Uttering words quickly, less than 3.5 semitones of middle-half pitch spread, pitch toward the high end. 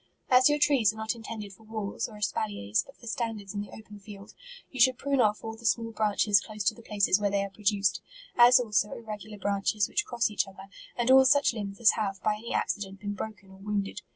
Yes: fast, 235 wpm; narrow, 2.5 semitones; high, 210 Hz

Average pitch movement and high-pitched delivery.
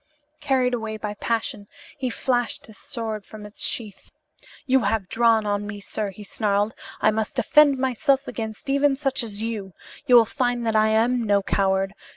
Yes: average, 3.2 semitones; high, 225 Hz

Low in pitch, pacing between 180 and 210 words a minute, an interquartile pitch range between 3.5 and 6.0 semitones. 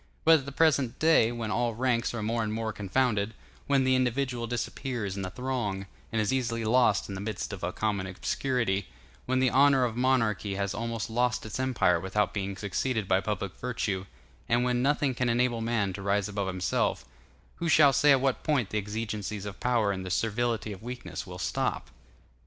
Yes: low, 115 Hz; average, 200 wpm; average, 3.9 semitones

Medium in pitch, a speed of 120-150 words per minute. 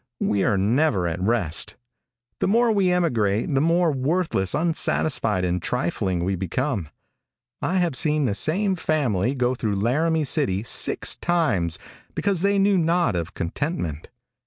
No: low, 130 Hz; average, 145 wpm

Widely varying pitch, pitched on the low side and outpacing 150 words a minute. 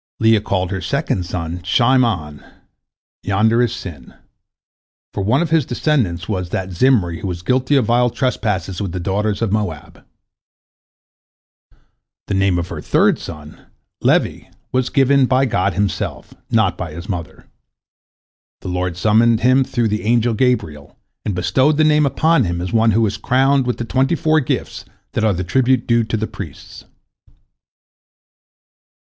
Yes: wide, 5.7 semitones; low, 110 Hz; average, 160 wpm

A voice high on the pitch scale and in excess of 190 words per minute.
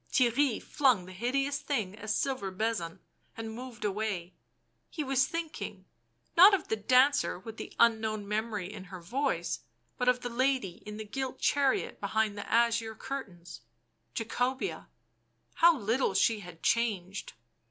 No: high, 225 Hz; average, 150 wpm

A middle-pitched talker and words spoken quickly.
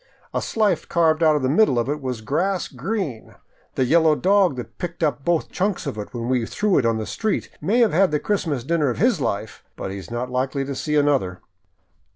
Yes: medium, 150 Hz; fast, 225 wpm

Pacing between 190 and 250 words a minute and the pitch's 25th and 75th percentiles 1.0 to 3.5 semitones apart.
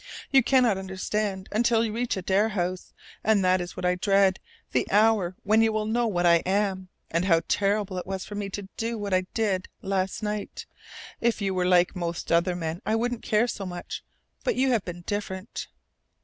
Yes: average, 200 wpm; average, 2.8 semitones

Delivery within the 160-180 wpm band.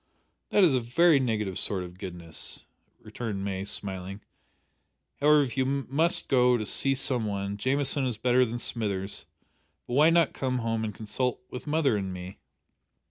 Yes: average, 165 wpm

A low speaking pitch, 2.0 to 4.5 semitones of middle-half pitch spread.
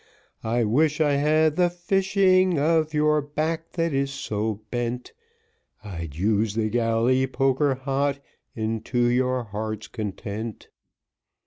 No: low, 130 Hz; wide, 5.5 semitones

